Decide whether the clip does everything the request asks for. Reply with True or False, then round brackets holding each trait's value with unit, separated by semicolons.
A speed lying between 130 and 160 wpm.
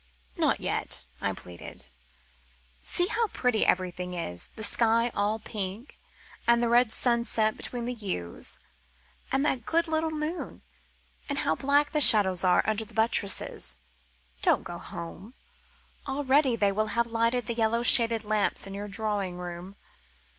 True (145 wpm)